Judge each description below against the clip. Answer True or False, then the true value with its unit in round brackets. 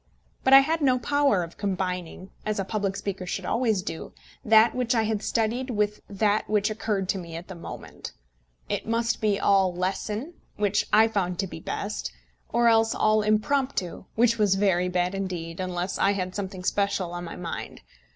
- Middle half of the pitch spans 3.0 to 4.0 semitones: True (3.3 semitones)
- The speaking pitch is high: True (205 Hz)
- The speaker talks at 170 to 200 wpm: True (185 wpm)